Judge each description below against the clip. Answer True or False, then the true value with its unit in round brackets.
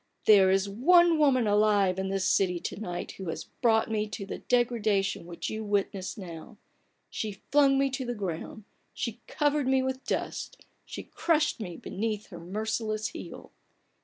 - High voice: True (215 Hz)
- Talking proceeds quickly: False (165 wpm)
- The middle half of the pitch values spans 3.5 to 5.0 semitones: True (4.7 semitones)